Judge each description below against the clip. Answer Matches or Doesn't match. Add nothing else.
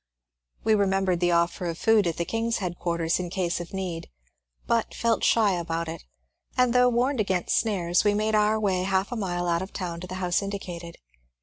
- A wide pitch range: Doesn't match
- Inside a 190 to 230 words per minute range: Matches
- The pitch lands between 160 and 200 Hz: Matches